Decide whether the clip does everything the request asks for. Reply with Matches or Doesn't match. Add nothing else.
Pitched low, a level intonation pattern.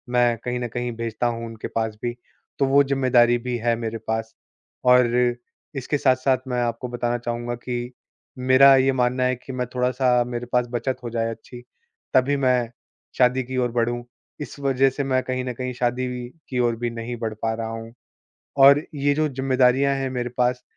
Matches